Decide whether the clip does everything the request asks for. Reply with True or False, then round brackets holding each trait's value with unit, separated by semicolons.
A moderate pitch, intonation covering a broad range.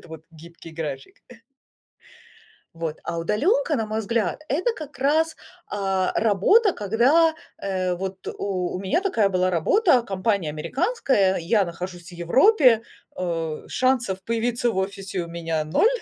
False (195 Hz; 6.7 semitones)